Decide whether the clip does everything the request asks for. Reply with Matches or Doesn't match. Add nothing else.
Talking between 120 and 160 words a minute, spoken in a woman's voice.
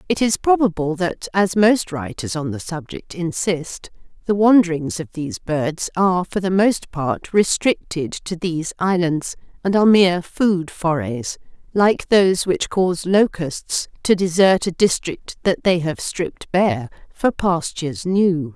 Matches